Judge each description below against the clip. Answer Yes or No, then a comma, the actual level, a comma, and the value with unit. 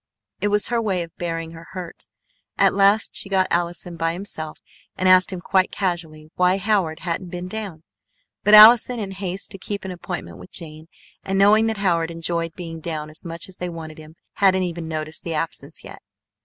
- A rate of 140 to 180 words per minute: No, average, 195 wpm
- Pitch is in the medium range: Yes, medium, 175 Hz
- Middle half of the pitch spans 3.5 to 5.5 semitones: No, average, 2.9 semitones